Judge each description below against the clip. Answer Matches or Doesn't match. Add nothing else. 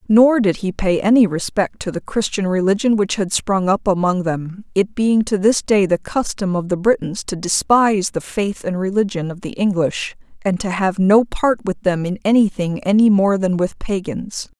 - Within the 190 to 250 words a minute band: Matches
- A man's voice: Doesn't match